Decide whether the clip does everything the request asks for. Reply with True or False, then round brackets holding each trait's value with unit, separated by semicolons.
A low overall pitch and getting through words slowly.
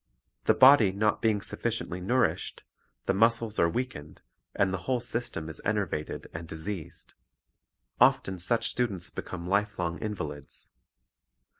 True (100 Hz; 125 wpm)